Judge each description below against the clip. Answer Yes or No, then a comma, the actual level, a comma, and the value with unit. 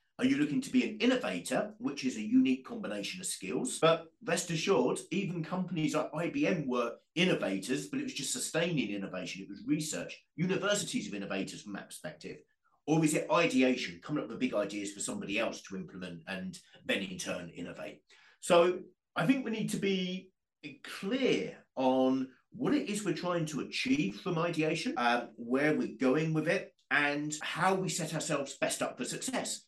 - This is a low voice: No, medium, 165 Hz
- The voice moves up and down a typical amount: No, wide, 7.1 semitones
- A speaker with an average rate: Yes, average, 180 wpm